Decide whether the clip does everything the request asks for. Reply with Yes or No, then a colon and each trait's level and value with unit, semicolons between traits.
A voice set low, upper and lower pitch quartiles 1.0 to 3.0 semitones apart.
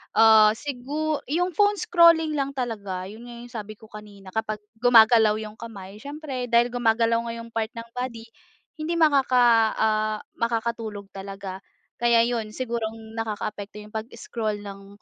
No: high, 230 Hz; narrow, 2.6 semitones